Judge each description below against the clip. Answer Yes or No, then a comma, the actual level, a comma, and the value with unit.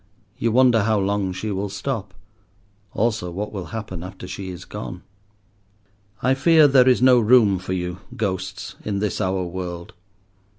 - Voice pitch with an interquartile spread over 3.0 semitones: Yes, average, 3.6 semitones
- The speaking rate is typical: Yes, average, 160 wpm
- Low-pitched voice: Yes, low, 100 Hz